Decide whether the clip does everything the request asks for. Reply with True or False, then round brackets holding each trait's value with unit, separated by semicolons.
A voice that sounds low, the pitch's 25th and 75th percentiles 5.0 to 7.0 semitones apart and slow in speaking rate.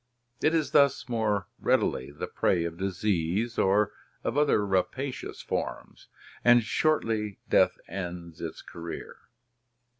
True (105 Hz; 5.5 semitones; 125 wpm)